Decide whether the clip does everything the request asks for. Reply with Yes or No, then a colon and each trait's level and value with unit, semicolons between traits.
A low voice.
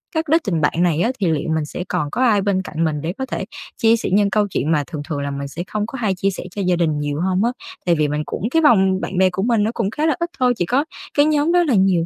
No: high, 190 Hz